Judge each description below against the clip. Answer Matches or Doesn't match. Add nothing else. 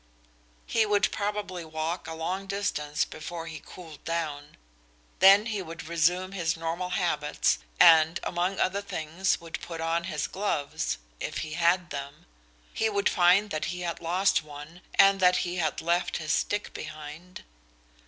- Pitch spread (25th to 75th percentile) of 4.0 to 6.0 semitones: Doesn't match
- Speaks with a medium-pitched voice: Matches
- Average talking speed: Matches